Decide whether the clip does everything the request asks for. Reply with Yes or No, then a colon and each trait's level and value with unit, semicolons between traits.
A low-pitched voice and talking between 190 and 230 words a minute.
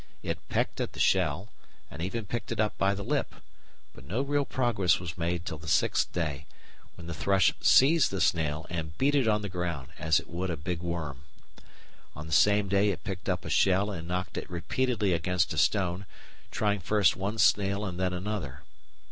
Yes: very low, 90 Hz; average, 200 wpm